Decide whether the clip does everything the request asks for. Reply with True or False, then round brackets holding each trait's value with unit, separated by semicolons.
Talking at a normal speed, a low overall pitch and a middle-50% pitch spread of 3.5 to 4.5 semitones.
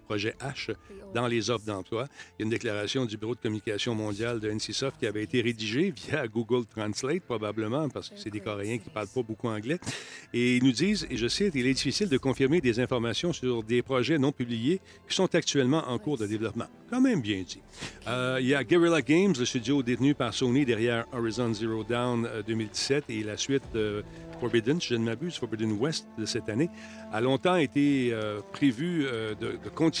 True (210 wpm; 120 Hz; 4.2 semitones)